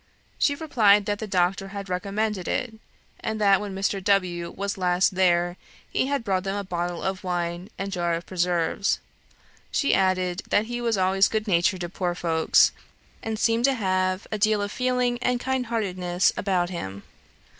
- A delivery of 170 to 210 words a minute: Yes, average, 175 wpm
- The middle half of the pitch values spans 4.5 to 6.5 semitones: No, average, 3.3 semitones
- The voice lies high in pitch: Yes, high, 195 Hz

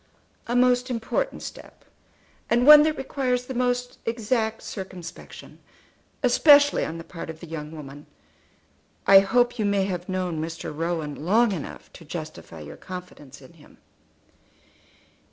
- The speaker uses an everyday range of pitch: No, wide, 7.2 semitones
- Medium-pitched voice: No, high, 195 Hz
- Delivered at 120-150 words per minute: Yes, average, 140 wpm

